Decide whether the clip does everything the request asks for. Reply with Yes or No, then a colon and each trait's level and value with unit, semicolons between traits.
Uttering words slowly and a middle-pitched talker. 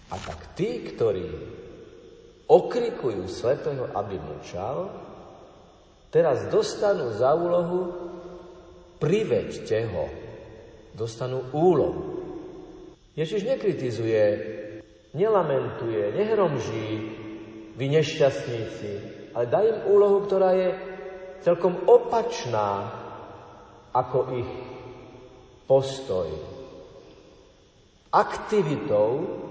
Yes: slow, 70 wpm; medium, 175 Hz